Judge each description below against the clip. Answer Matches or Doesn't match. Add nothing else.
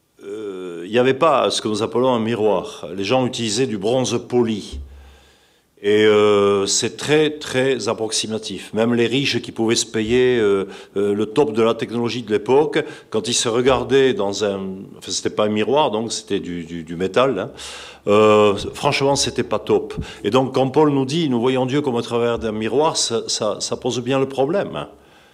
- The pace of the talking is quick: Doesn't match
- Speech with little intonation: Doesn't match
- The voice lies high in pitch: Doesn't match